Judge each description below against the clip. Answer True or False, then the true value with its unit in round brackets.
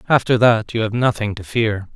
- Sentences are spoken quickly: True (215 wpm)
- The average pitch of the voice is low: True (110 Hz)